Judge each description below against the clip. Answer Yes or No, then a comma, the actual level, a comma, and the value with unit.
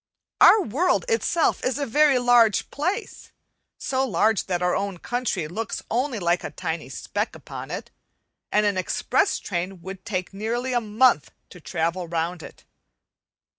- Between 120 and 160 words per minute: Yes, average, 155 wpm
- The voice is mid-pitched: No, high, 210 Hz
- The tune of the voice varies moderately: No, wide, 6.2 semitones